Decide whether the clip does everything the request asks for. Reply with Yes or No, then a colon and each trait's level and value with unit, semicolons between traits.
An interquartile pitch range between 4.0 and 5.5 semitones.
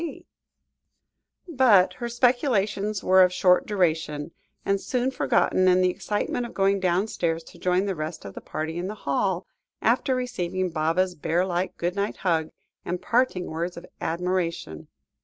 No: average, 3.4 semitones